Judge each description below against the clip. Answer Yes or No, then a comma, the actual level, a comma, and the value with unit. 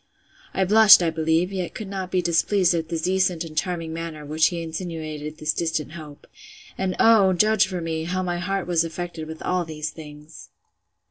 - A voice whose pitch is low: No, medium, 170 Hz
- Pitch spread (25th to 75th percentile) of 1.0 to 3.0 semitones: Yes, narrow, 2.6 semitones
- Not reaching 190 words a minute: No, average, 195 wpm